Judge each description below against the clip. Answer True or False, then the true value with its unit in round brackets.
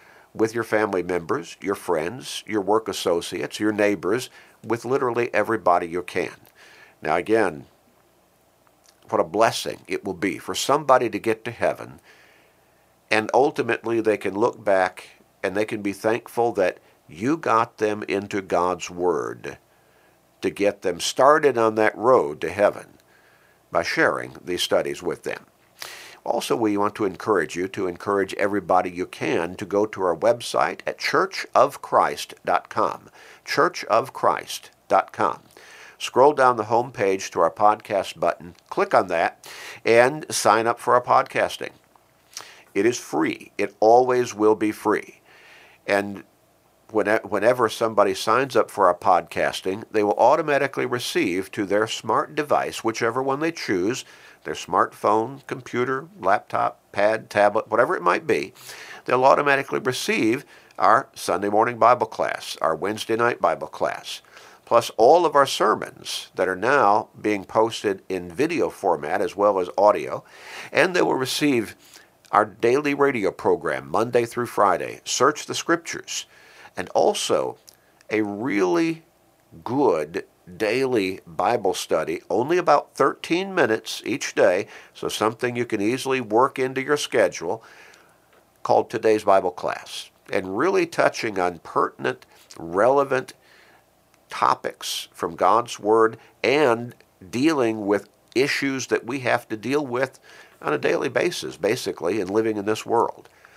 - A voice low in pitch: True (110 Hz)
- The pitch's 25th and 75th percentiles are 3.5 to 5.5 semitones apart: False (3.0 semitones)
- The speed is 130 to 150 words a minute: True (140 wpm)